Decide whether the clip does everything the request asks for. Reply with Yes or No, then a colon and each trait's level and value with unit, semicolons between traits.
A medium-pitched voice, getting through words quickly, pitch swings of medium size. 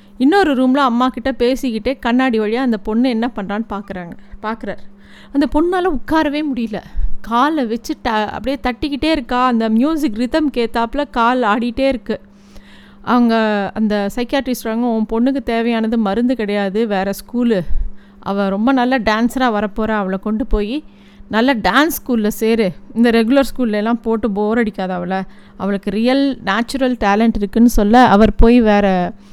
No: high, 230 Hz; fast, 140 wpm; average, 3.7 semitones